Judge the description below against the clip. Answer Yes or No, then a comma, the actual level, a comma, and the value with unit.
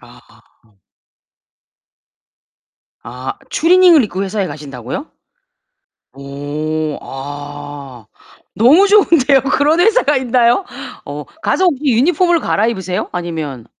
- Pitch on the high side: Yes, high, 195 Hz